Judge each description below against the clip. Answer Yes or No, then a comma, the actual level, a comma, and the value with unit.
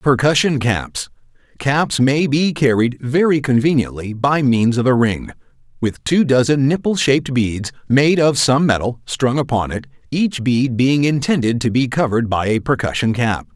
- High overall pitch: No, low, 130 Hz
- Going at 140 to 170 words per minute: Yes, average, 160 wpm